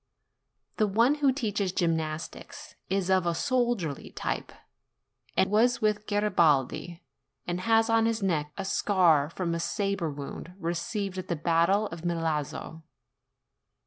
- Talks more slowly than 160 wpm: Yes, slow, 135 wpm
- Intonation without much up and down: No, average, 4.4 semitones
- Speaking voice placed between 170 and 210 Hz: Yes, medium, 185 Hz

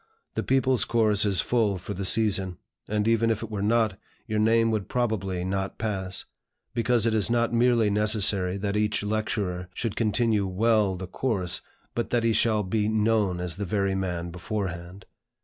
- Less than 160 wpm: No, average, 175 wpm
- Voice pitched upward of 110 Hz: No, low, 105 Hz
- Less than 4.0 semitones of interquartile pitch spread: Yes, average, 2.9 semitones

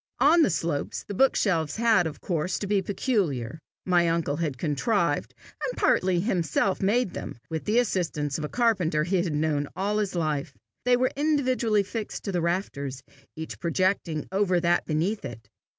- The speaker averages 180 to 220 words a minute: No, average, 170 wpm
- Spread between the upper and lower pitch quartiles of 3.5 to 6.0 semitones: Yes, average, 5.0 semitones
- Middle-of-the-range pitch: Yes, medium, 180 Hz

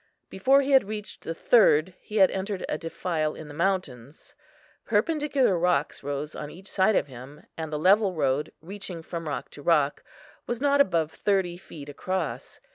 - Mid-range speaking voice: Yes, medium, 175 Hz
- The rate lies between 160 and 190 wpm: Yes, average, 175 wpm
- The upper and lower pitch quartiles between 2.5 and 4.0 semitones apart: No, average, 5.2 semitones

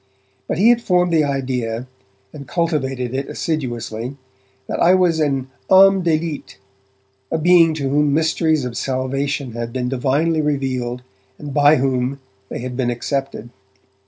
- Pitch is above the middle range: No, medium, 140 Hz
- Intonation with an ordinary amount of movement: Yes, average, 3.9 semitones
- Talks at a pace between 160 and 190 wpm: No, average, 150 wpm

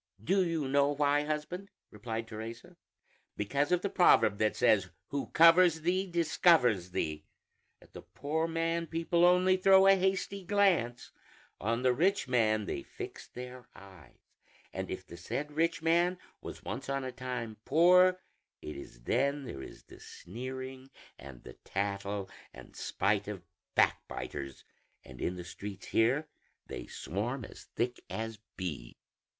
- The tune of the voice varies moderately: No, wide, 7.9 semitones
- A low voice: Yes, low, 130 Hz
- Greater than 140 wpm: Yes, average, 150 wpm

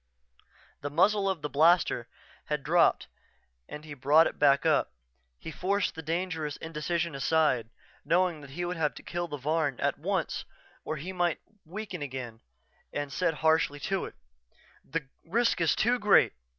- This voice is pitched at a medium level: Yes, medium, 160 Hz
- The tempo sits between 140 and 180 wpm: Yes, average, 160 wpm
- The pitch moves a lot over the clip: No, average, 3.3 semitones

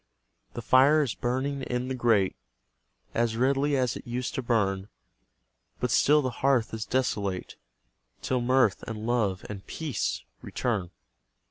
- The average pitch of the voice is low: Yes, low, 120 Hz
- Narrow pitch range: No, average, 3.3 semitones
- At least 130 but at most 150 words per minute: Yes, average, 140 wpm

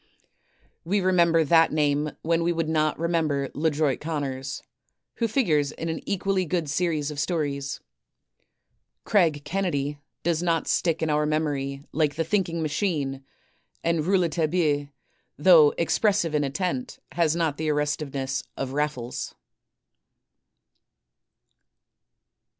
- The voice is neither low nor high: Yes, medium, 155 Hz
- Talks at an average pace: No, slow, 115 wpm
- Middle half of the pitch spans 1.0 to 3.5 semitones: Yes, average, 2.8 semitones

